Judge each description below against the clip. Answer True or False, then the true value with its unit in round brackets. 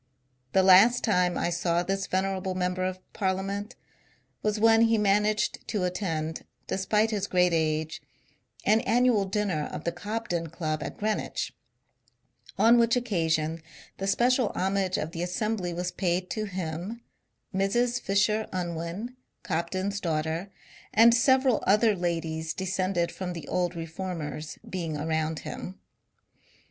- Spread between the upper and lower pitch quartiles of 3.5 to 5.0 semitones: True (3.8 semitones)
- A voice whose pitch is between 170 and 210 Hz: True (185 Hz)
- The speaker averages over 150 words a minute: False (135 wpm)